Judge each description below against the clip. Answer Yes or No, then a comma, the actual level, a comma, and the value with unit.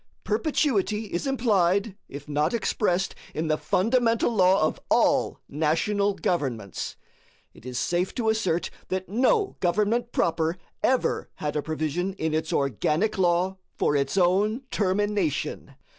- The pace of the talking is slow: Yes, slow, 130 wpm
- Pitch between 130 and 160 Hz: No, medium, 185 Hz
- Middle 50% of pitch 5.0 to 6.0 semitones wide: Yes, average, 5.3 semitones